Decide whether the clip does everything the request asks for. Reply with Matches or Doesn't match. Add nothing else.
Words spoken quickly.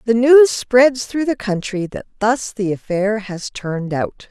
Doesn't match